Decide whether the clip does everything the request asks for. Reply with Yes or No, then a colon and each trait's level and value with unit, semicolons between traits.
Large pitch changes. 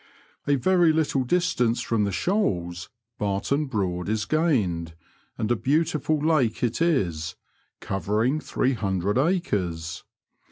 Yes: wide, 8.2 semitones